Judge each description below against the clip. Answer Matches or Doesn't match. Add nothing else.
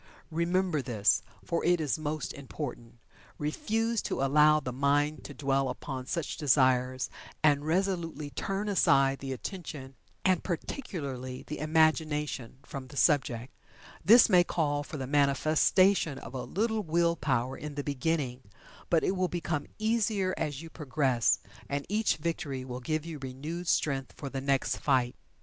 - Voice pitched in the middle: Matches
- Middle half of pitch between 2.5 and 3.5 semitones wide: Doesn't match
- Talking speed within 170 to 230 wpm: Doesn't match